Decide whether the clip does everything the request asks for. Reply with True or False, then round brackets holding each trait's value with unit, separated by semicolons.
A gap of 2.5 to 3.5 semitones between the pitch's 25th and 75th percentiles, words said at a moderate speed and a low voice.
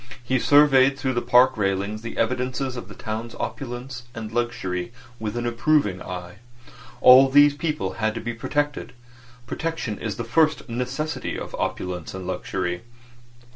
False (3.9 semitones; 150 wpm; 120 Hz)